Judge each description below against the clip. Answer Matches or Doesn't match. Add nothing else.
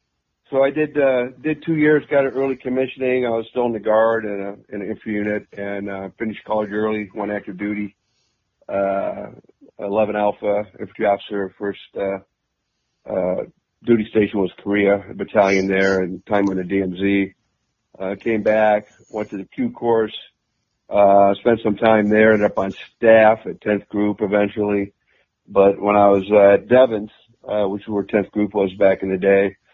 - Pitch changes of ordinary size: Doesn't match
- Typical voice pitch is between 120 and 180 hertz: Doesn't match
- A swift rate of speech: Doesn't match